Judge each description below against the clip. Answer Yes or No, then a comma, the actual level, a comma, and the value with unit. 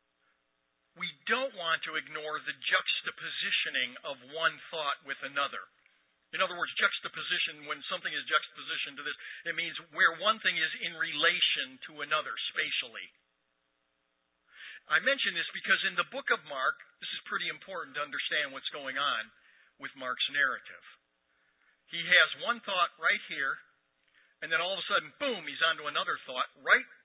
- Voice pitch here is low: No, medium, 150 Hz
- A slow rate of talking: No, average, 160 wpm